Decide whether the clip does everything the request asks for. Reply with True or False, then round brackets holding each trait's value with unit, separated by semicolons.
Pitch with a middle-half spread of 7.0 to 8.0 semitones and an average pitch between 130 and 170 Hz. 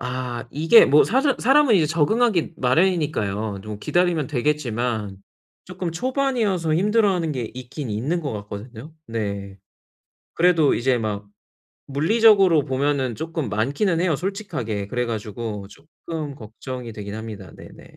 True (7.7 semitones; 140 Hz)